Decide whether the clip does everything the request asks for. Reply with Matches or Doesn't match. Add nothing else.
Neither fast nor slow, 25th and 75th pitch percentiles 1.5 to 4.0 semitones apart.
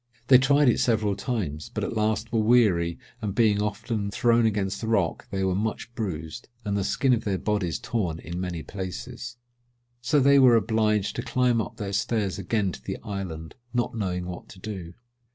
Matches